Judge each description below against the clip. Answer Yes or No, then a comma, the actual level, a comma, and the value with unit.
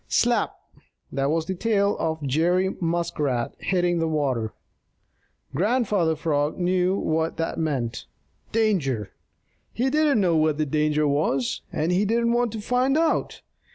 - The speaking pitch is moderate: Yes, medium, 165 Hz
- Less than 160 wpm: Yes, average, 140 wpm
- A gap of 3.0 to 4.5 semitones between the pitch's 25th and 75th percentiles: No, wide, 5.4 semitones